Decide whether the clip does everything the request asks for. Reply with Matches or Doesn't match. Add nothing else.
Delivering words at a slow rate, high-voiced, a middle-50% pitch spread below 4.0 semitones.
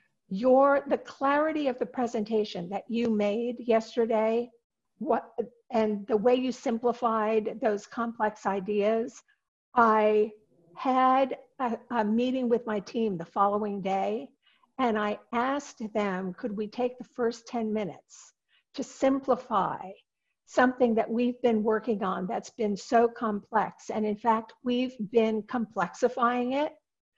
Matches